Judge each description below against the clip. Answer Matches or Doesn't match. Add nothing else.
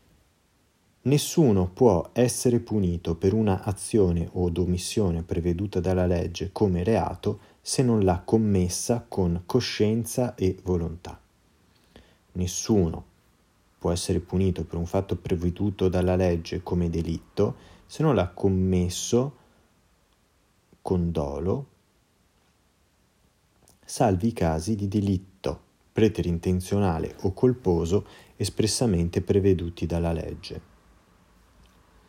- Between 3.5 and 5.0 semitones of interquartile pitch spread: Doesn't match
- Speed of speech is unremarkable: Doesn't match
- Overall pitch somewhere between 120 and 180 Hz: Doesn't match